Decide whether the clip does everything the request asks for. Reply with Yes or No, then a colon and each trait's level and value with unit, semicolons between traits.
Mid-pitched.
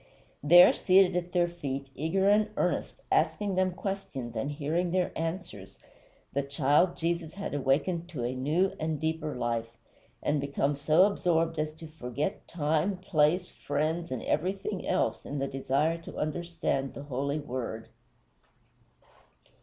Yes: medium, 155 Hz